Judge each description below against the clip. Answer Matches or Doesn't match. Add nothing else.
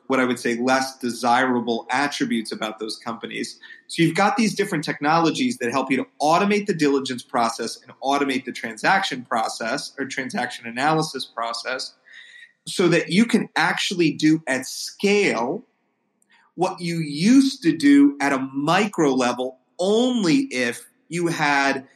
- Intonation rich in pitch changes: Matches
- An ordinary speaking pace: Matches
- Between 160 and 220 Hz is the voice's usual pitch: Doesn't match